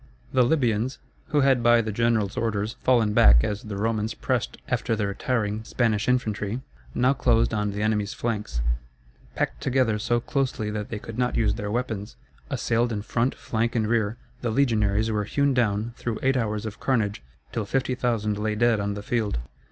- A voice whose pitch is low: Yes, low, 110 Hz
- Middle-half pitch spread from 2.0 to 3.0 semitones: Yes, narrow, 2.5 semitones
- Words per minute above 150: Yes, average, 180 wpm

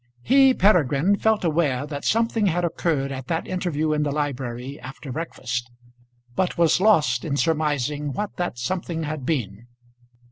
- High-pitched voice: No, medium, 150 Hz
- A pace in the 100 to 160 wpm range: Yes, average, 150 wpm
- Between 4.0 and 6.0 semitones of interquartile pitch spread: Yes, average, 4.7 semitones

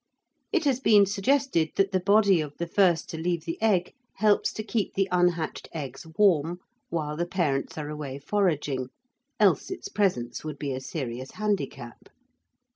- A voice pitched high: No, medium, 175 Hz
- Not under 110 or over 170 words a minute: Yes, average, 165 wpm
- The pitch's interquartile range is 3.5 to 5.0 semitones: No, wide, 5.4 semitones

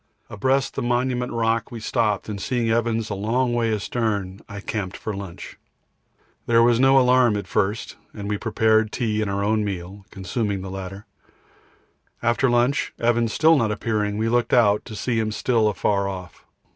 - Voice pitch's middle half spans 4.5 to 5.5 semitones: No, average, 2.9 semitones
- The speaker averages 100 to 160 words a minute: No, average, 180 wpm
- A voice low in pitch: Yes, low, 110 Hz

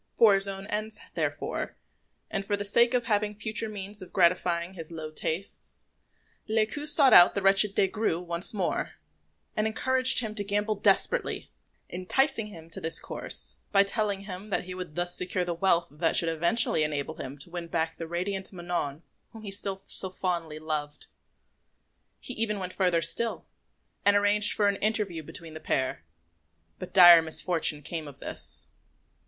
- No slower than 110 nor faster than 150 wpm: No, average, 170 wpm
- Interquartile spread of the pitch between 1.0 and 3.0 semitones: No, average, 3.8 semitones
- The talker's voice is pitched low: No, high, 190 Hz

